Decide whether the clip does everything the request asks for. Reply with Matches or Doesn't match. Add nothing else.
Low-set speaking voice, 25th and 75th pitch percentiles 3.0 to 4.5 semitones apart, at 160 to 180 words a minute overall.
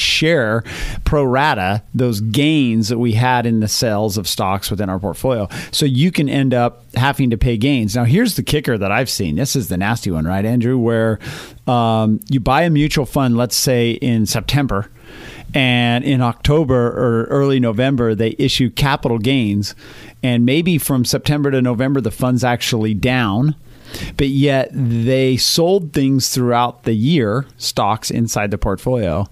Matches